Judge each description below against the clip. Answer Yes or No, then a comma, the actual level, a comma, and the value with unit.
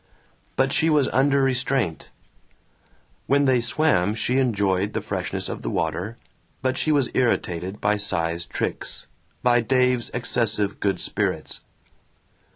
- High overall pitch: No, low, 120 Hz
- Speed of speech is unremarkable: No, slow, 130 wpm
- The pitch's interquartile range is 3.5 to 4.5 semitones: No, average, 4.9 semitones